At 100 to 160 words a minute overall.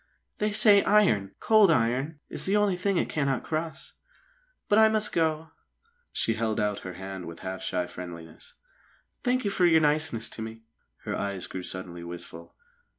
No: average, 170 wpm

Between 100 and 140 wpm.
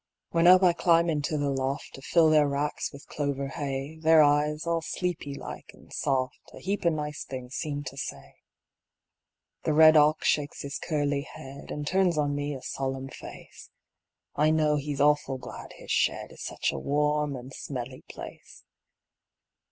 No: average, 175 wpm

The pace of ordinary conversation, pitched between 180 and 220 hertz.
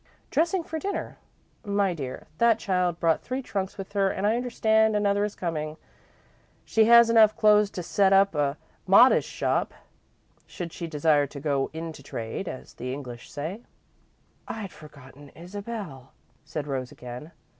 Yes: average, 155 wpm; medium, 185 Hz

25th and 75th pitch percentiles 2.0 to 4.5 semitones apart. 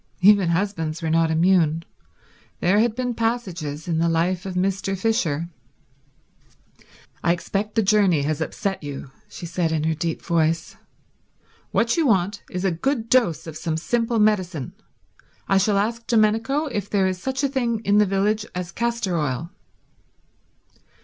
No: average, 5.0 semitones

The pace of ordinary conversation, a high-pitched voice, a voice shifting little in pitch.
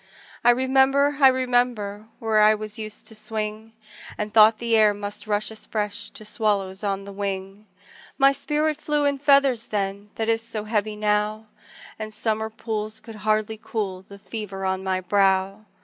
Yes: average, 170 wpm; high, 215 Hz; narrow, 2.1 semitones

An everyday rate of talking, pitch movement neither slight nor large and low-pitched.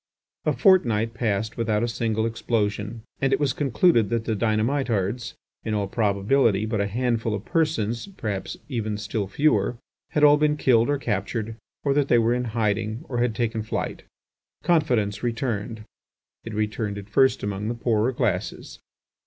Yes: average, 160 wpm; average, 3.0 semitones; low, 115 Hz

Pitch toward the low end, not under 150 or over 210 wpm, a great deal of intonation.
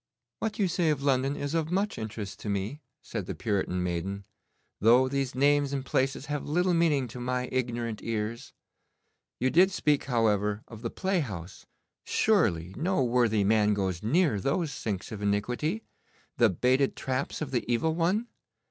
Yes: low, 125 Hz; average, 165 wpm; wide, 5.9 semitones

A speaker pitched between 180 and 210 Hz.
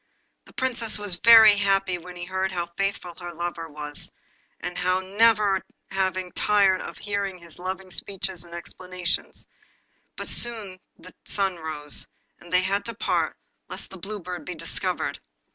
Yes: medium, 185 Hz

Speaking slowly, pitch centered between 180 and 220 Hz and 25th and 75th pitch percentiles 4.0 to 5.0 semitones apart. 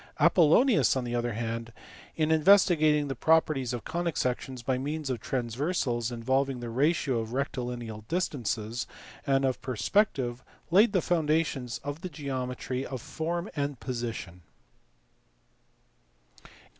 No: slow, 125 wpm; low, 135 Hz; average, 4.6 semitones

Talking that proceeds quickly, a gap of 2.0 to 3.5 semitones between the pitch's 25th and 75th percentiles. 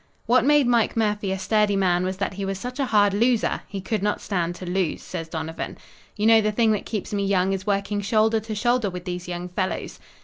Yes: fast, 235 wpm; average, 2.9 semitones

